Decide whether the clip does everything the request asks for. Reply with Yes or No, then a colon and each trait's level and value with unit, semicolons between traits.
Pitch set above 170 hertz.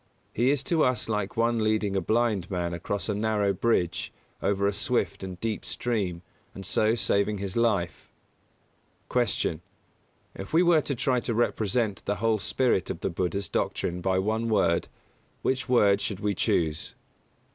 No: low, 105 Hz